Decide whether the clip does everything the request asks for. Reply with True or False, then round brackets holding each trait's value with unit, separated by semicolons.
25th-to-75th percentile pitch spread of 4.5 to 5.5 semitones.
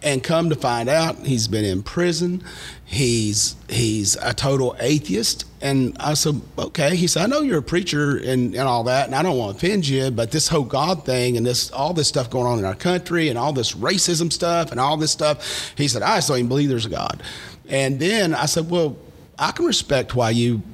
True (5.1 semitones)